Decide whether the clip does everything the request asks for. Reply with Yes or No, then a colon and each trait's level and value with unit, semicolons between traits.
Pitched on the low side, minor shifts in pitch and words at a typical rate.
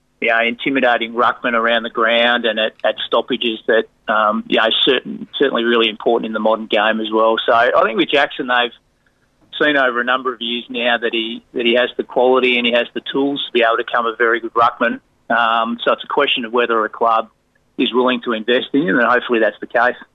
No: low, 120 Hz; narrow, 1.3 semitones; fast, 240 wpm